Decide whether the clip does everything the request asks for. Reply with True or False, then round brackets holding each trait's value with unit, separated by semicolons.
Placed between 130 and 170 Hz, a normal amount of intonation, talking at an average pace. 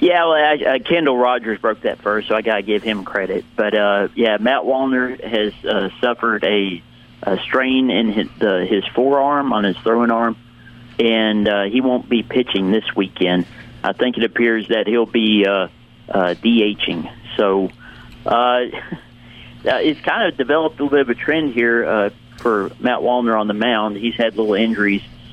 False (115 Hz; 3.2 semitones; 180 wpm)